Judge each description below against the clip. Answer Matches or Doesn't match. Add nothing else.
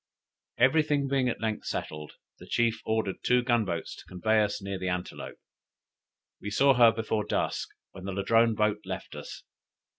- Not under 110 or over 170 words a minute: Doesn't match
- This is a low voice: Matches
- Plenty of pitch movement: Doesn't match